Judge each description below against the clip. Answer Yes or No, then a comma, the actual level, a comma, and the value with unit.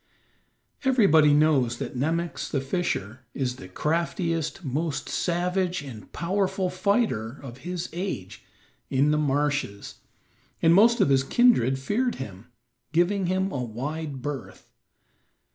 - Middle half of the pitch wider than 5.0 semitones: Yes, wide, 5.4 semitones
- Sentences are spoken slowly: Yes, slow, 125 wpm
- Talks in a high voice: No, medium, 155 Hz